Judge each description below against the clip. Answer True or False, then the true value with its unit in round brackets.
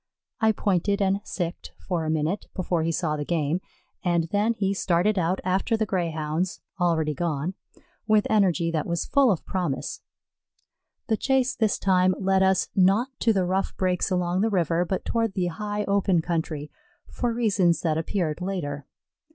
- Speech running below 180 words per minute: True (170 wpm)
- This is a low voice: False (185 Hz)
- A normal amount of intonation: True (3.2 semitones)